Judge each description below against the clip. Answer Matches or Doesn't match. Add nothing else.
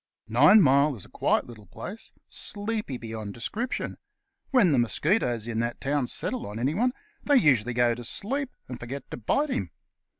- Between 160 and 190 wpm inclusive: Matches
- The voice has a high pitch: Doesn't match